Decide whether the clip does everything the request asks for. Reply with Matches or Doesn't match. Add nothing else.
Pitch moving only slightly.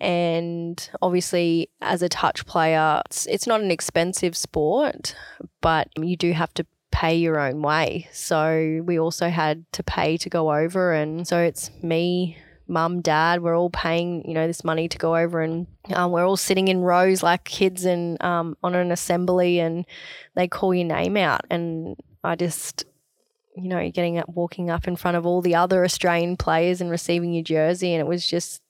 Matches